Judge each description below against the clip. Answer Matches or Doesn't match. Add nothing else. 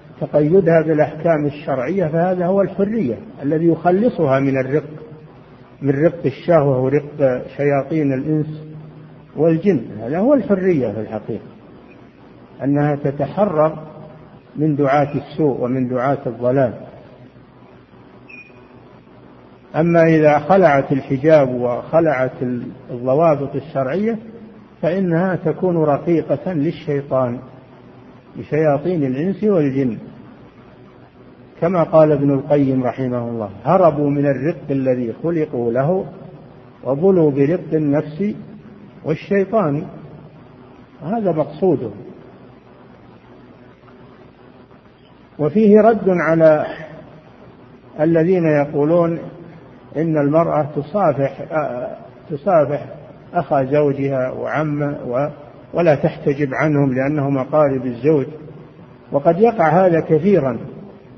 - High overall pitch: Doesn't match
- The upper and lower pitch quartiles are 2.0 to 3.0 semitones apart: Doesn't match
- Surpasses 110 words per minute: Doesn't match